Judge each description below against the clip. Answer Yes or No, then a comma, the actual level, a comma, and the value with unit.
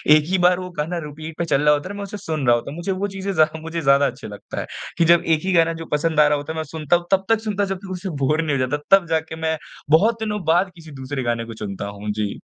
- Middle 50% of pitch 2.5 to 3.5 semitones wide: No, average, 4.1 semitones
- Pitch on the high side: No, medium, 160 Hz